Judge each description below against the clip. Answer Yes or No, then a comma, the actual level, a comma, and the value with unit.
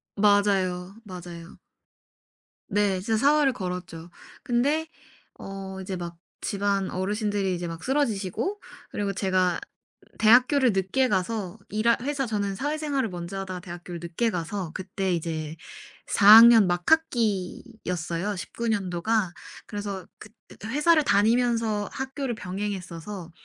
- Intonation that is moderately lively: Yes, average, 4.2 semitones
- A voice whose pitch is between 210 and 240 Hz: No, high, 200 Hz